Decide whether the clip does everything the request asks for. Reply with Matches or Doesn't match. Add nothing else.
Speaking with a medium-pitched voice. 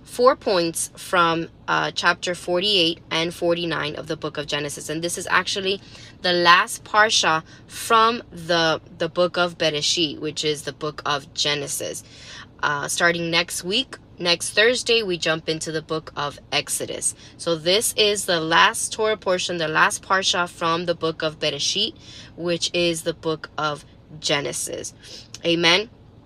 Matches